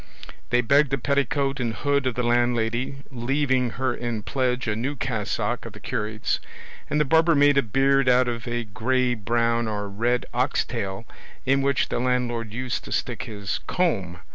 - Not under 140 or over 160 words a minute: No, average, 180 wpm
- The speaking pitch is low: Yes, low, 125 Hz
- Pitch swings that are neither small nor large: Yes, average, 3.1 semitones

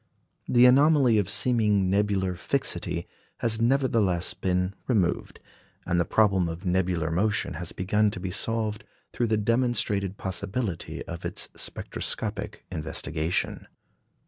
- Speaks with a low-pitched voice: Yes, low, 100 Hz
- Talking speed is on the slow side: Yes, slow, 120 wpm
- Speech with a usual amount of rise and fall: Yes, average, 4.0 semitones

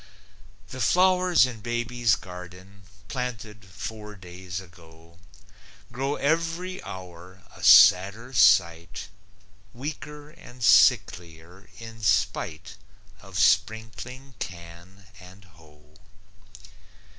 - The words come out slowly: Yes, slow, 85 wpm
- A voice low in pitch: Yes, low, 100 Hz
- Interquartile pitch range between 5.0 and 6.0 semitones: Yes, wide, 5.5 semitones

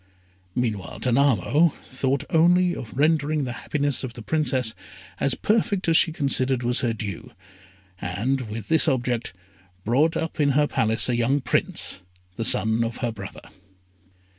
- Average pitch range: Yes, average, 4.5 semitones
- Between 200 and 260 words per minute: No, average, 150 wpm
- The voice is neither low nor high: No, low, 130 Hz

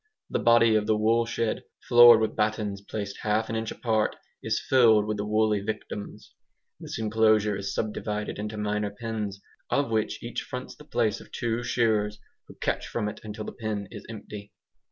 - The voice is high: No, low, 110 Hz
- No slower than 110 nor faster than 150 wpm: No, average, 175 wpm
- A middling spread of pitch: No, narrow, 1.3 semitones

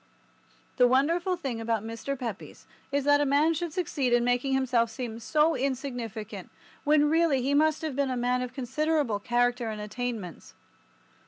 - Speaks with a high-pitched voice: Yes, very high, 260 Hz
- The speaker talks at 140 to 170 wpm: Yes, average, 165 wpm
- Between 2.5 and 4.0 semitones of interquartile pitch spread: Yes, average, 3.5 semitones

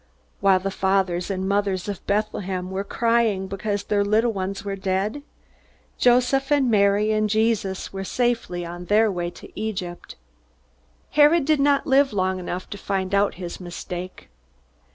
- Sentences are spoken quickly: No, average, 155 wpm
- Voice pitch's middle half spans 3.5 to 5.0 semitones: No, average, 3.0 semitones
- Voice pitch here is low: No, high, 200 Hz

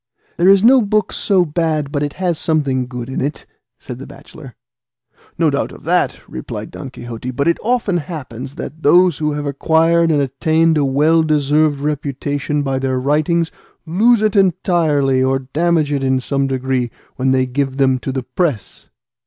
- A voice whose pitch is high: No, medium, 145 Hz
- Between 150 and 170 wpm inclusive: No, average, 180 wpm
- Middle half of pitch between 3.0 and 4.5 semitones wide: Yes, average, 3.7 semitones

